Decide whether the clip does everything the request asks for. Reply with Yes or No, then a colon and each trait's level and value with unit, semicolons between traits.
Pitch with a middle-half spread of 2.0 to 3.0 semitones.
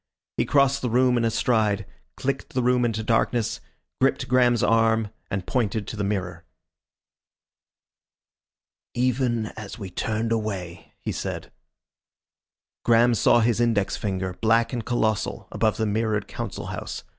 Yes: narrow, 2.5 semitones